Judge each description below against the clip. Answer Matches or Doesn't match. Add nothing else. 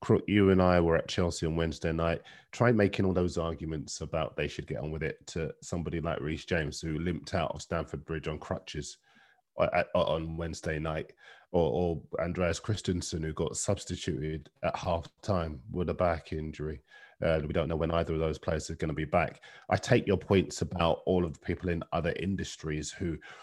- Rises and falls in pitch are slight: Matches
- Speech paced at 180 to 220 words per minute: Matches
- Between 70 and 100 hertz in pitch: Matches